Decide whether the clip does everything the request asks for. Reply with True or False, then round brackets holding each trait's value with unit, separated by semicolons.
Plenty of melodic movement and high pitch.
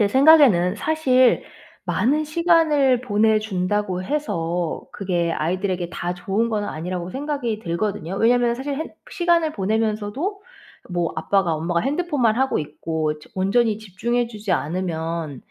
True (6.9 semitones; 210 Hz)